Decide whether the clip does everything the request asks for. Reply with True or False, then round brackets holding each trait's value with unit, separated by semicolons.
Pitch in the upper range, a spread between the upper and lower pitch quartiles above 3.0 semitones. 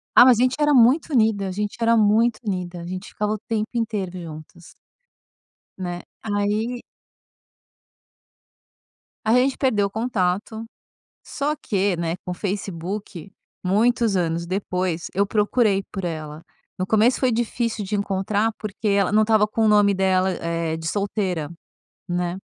True (205 Hz; 3.5 semitones)